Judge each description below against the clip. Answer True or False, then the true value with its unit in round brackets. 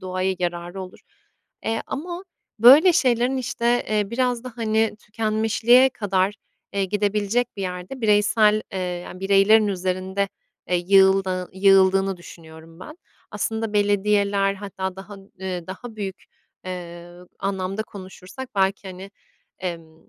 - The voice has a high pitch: True (195 Hz)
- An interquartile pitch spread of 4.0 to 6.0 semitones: False (2.8 semitones)